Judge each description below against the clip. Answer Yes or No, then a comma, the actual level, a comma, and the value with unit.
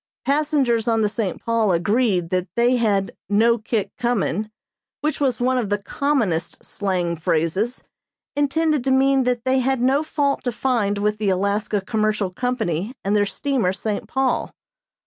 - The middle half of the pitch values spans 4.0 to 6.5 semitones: Yes, average, 4.3 semitones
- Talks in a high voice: Yes, high, 225 Hz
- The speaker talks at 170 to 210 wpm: No, average, 160 wpm